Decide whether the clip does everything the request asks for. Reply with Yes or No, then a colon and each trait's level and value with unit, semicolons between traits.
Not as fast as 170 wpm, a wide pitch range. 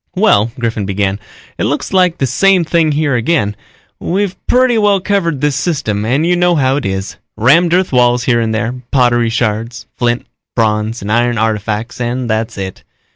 No: average, 180 wpm; wide, 7.2 semitones